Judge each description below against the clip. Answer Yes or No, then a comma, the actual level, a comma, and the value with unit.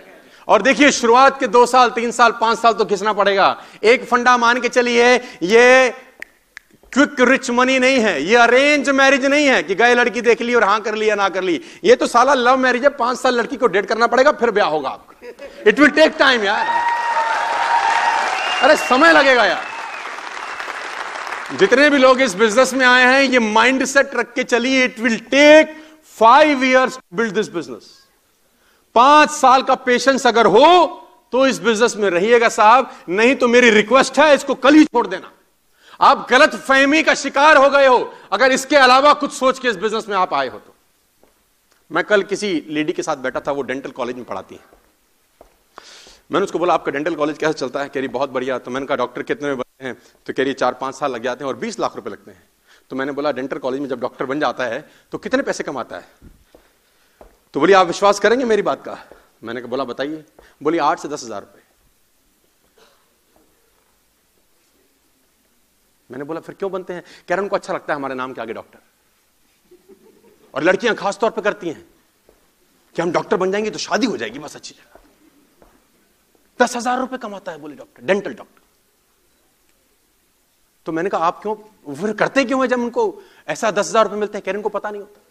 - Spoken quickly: Yes, fast, 200 wpm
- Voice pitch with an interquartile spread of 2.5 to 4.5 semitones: No, wide, 5.4 semitones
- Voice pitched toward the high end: Yes, high, 240 Hz